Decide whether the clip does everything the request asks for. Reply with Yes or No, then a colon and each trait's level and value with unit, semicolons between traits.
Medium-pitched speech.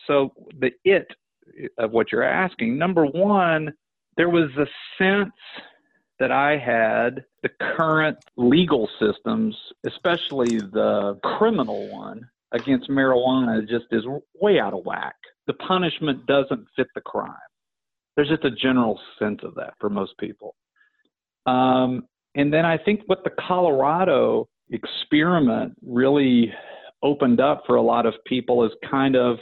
Yes: medium, 145 Hz